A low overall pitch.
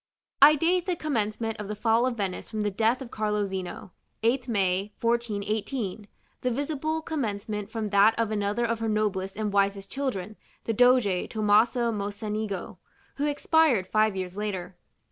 No: high, 215 Hz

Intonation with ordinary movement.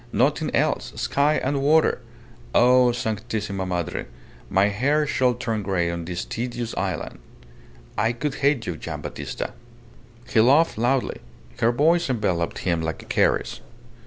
No: wide, 5.8 semitones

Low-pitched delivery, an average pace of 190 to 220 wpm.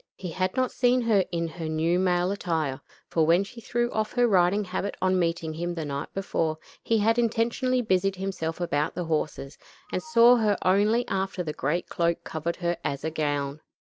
No: medium, 180 Hz; average, 195 wpm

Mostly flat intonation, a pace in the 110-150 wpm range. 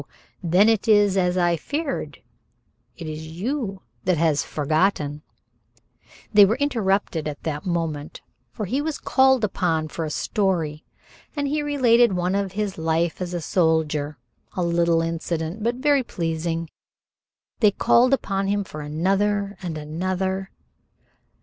No: average, 4.6 semitones; average, 140 wpm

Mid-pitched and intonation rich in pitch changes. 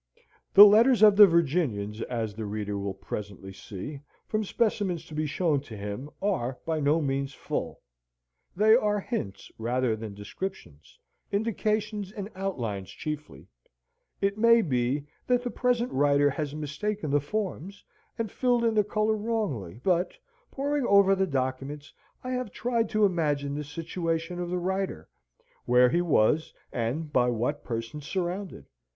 Yes: medium, 160 Hz; wide, 8.4 semitones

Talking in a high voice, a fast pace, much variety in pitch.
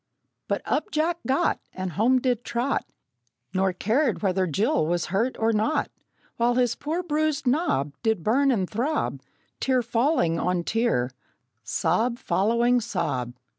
No: high, 235 Hz; average, 140 wpm; wide, 5.9 semitones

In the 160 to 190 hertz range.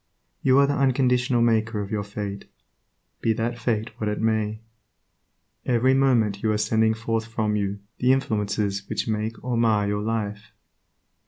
No: low, 110 Hz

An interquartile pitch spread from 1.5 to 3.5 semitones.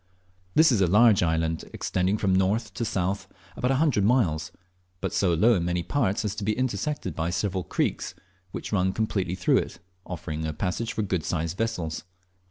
No: average, 4.2 semitones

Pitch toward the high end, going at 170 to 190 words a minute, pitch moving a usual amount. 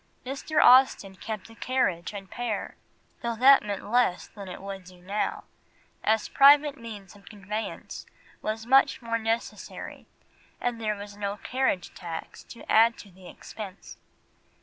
No: high, 215 Hz; average, 150 wpm; average, 3.5 semitones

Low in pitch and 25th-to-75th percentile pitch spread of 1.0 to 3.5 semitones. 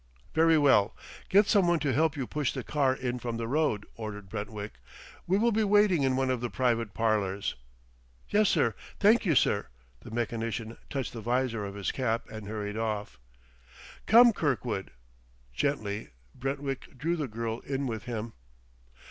No: low, 125 Hz; average, 5.3 semitones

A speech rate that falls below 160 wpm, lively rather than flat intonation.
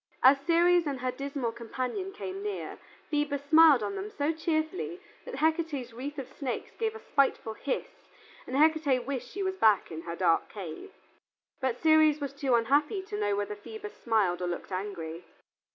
No: average, 175 wpm; wide, 6.2 semitones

